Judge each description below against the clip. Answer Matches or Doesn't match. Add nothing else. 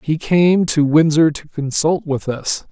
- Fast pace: Doesn't match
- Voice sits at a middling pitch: Matches